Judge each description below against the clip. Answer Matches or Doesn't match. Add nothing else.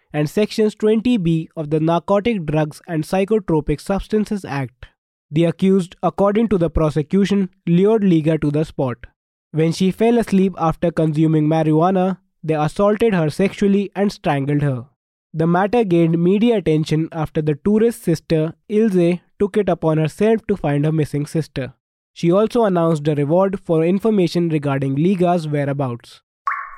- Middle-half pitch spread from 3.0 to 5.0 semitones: Matches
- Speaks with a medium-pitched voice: Matches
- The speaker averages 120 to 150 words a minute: Matches